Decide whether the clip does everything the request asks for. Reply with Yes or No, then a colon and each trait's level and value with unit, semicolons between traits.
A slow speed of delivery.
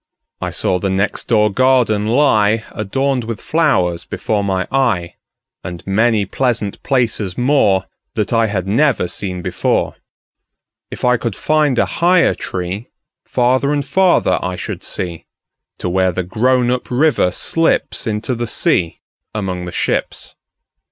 Yes: slow, 125 wpm